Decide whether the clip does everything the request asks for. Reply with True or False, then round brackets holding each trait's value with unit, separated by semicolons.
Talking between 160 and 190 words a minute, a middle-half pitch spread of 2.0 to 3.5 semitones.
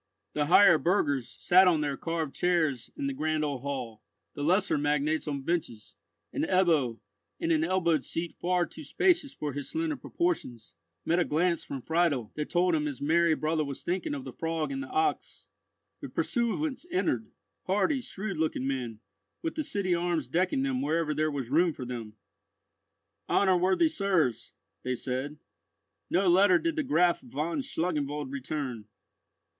False (165 wpm; 4.9 semitones)